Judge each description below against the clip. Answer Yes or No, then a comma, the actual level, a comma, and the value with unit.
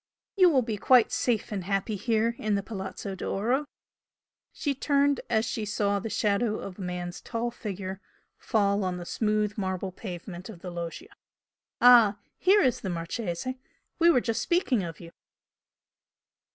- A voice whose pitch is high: Yes, high, 210 Hz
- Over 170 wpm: No, average, 160 wpm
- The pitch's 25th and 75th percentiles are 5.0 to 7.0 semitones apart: No, average, 4.2 semitones